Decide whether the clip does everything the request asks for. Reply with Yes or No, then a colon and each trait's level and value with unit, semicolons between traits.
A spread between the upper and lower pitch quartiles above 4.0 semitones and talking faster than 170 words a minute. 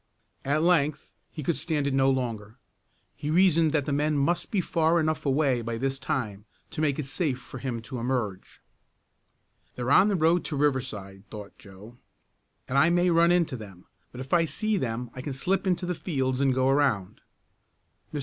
Yes: average, 4.4 semitones; average, 190 wpm